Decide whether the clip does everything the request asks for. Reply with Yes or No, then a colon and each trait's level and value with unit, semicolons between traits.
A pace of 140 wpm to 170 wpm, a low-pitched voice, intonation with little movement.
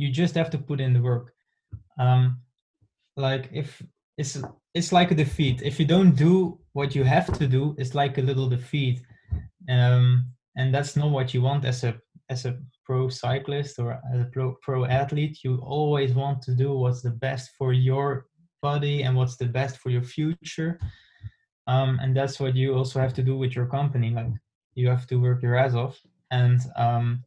No: average, 195 wpm; low, 130 Hz; narrow, 2.1 semitones